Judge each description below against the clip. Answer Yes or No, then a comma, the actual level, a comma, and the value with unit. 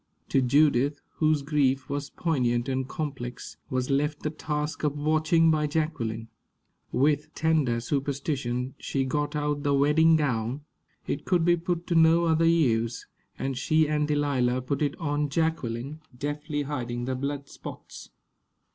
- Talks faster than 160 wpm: No, average, 145 wpm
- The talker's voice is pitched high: No, medium, 145 Hz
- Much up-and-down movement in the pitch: No, average, 3.0 semitones